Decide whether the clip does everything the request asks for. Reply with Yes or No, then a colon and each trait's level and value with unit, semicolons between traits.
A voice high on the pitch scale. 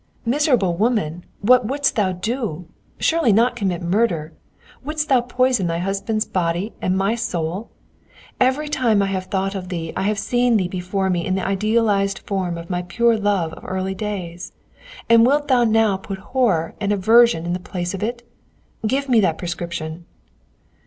Yes: high, 200 Hz